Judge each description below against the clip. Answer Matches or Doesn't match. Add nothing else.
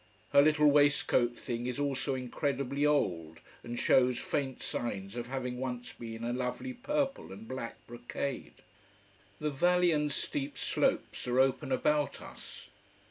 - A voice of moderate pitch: Doesn't match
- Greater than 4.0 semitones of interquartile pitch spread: Doesn't match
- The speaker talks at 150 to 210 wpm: Doesn't match